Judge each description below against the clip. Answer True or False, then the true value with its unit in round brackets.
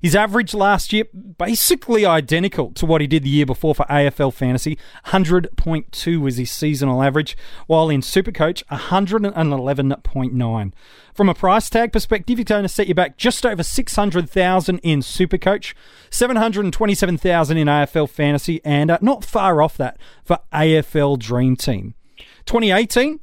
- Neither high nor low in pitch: True (170 Hz)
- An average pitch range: False (6.0 semitones)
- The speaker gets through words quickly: False (140 wpm)